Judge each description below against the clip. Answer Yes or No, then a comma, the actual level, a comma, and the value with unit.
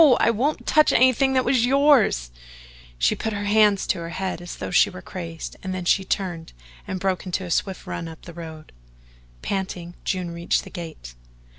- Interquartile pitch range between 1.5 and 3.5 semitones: No, average, 4.5 semitones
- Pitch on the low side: No, medium, 185 Hz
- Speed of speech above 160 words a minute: Yes, average, 190 wpm